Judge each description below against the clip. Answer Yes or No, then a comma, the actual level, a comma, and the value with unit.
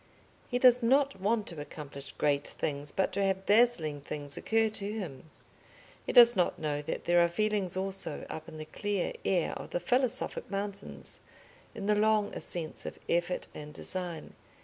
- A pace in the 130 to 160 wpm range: No, average, 170 wpm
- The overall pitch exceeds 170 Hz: Yes, high, 190 Hz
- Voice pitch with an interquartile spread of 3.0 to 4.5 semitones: No, wide, 5.4 semitones